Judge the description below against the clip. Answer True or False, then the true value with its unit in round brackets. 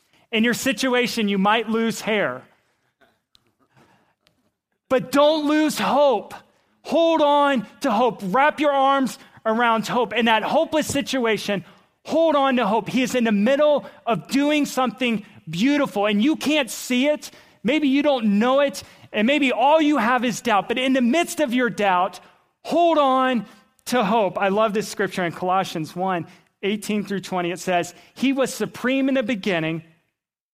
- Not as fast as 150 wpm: False (165 wpm)